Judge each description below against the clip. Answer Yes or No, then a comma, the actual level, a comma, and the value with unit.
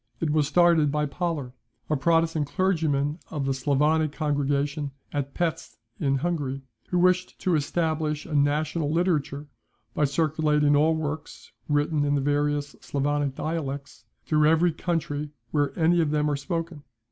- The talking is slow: No, average, 145 wpm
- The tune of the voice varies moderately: No, narrow, 2.1 semitones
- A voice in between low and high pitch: Yes, medium, 150 Hz